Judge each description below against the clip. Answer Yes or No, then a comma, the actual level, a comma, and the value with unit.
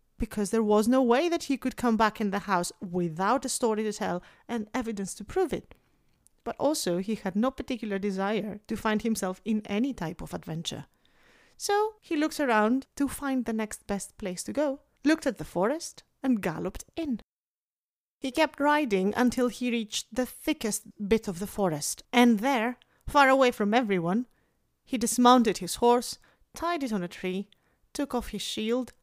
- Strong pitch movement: No, average, 4.5 semitones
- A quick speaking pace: No, average, 180 wpm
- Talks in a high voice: Yes, high, 230 Hz